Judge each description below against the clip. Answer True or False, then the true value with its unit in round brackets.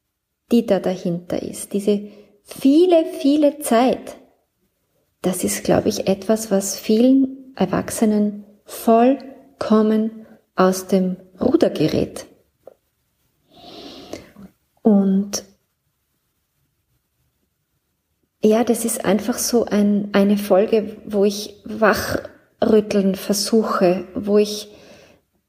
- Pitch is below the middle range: False (215 Hz)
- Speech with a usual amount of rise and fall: True (3.0 semitones)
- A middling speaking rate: False (85 wpm)